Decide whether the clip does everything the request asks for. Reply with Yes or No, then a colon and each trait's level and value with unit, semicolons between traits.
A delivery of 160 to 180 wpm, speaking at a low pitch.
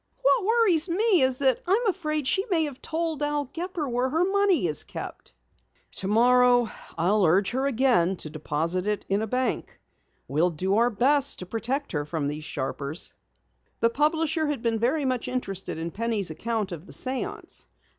No: average, 175 wpm; very high, 250 Hz